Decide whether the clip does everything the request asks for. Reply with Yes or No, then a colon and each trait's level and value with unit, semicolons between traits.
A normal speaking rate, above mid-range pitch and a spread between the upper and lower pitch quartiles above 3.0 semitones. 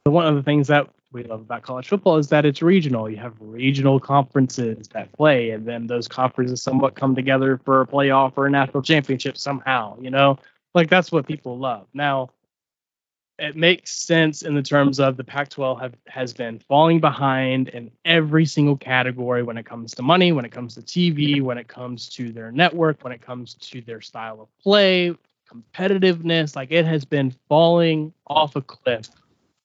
No: average, 190 wpm; low, 135 Hz; average, 3.7 semitones